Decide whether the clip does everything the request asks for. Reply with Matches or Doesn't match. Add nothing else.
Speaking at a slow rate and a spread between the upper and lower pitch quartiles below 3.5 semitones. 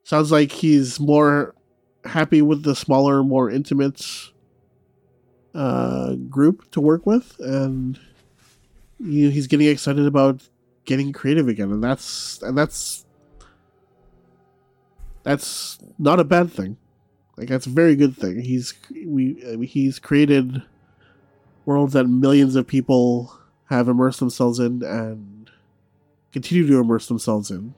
Matches